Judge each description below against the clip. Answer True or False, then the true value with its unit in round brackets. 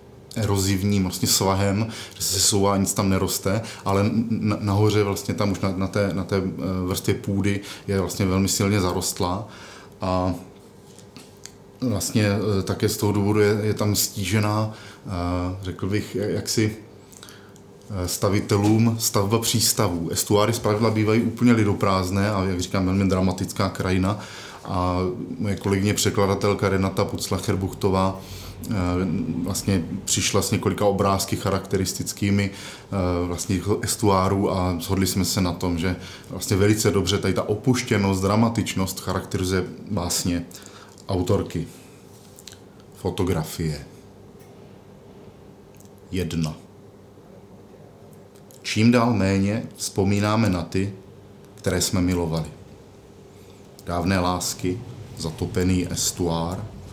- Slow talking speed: True (105 wpm)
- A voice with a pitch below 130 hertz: True (100 Hz)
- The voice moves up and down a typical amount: False (1.9 semitones)